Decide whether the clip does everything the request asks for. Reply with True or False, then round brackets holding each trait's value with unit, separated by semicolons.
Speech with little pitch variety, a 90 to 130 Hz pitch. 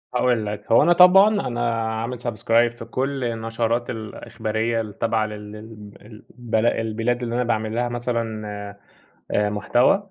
True (1.9 semitones; 115 Hz)